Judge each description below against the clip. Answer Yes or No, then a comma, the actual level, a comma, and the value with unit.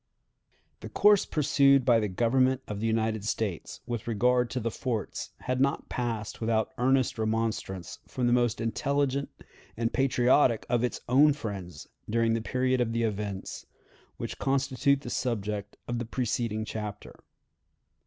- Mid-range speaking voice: No, low, 120 Hz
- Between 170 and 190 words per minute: No, average, 150 wpm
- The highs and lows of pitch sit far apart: No, average, 2.8 semitones